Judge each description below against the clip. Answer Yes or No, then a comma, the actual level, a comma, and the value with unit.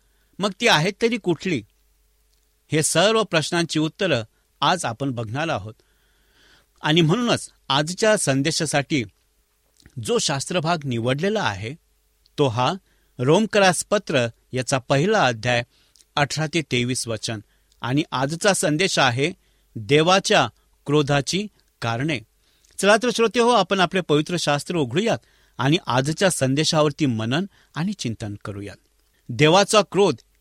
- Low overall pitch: No, medium, 150 Hz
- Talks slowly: Yes, slow, 110 wpm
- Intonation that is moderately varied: No, wide, 7.1 semitones